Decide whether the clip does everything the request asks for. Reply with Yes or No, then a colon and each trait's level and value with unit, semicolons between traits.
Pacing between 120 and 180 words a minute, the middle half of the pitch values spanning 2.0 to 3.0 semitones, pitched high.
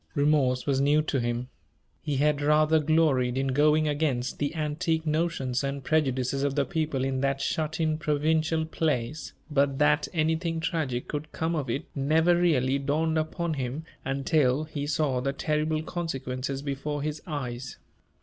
No: average, 160 wpm; narrow, 2.6 semitones; medium, 150 Hz